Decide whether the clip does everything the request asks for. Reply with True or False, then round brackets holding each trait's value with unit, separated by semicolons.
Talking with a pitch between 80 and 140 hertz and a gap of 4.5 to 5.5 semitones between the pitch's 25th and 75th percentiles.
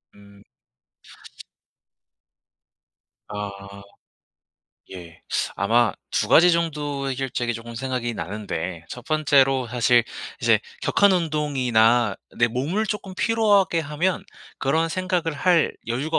False (135 Hz; 6.0 semitones)